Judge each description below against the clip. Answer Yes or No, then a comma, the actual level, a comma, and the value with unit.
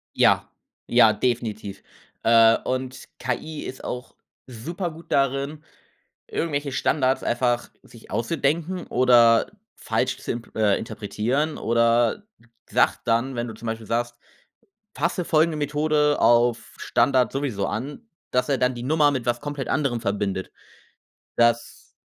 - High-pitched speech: No, low, 125 Hz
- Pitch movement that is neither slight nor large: Yes, average, 3.8 semitones